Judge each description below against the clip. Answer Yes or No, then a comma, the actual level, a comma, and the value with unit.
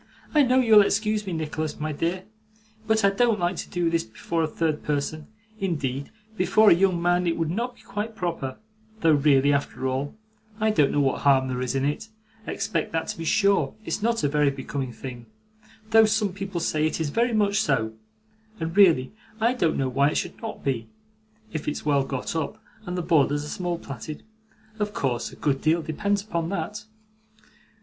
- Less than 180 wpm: No, average, 200 wpm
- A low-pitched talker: No, medium, 165 Hz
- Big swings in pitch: Yes, wide, 6.0 semitones